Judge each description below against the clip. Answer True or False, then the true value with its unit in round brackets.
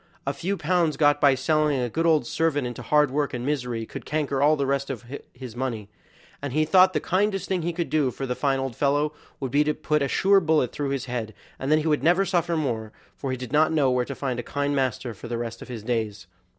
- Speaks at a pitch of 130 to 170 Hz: True (140 Hz)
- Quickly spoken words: True (255 wpm)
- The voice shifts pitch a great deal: False (3.7 semitones)